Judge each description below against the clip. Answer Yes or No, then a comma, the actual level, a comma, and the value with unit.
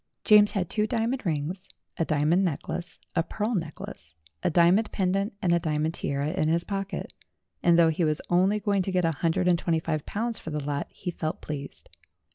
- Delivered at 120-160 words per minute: No, fast, 205 wpm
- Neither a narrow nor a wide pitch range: Yes, average, 3.9 semitones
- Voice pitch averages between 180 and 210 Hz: No, medium, 170 Hz